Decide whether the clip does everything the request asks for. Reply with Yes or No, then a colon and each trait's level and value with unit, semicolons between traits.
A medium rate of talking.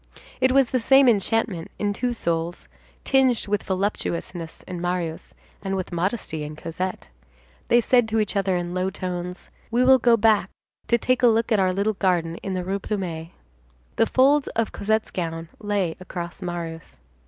Yes: average, 175 wpm